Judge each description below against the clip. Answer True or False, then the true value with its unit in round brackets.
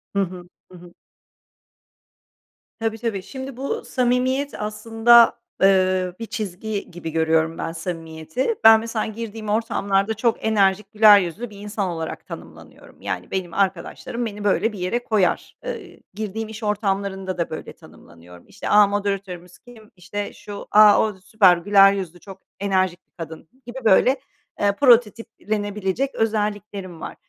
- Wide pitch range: False (3.4 semitones)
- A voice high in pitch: True (205 Hz)